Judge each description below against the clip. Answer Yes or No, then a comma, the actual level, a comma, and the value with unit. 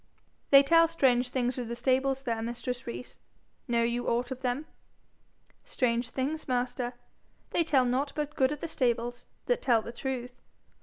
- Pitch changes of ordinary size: No, narrow, 2.2 semitones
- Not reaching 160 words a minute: No, average, 165 wpm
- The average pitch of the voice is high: Yes, very high, 250 Hz